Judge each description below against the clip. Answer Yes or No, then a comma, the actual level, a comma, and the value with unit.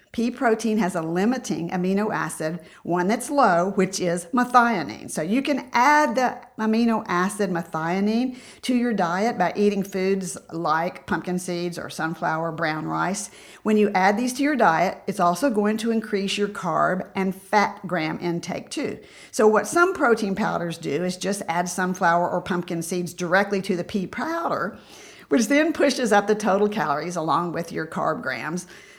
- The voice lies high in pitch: Yes, high, 195 Hz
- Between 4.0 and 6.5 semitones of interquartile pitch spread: Yes, average, 4.5 semitones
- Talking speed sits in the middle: Yes, average, 170 wpm